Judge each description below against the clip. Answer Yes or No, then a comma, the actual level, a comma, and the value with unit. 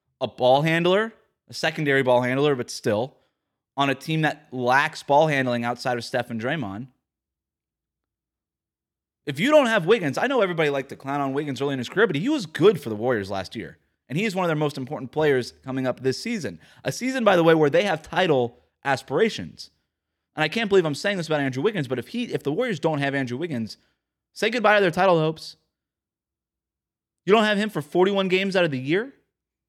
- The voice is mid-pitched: Yes, medium, 145 Hz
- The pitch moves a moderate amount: No, wide, 6.7 semitones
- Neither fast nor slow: No, fast, 215 wpm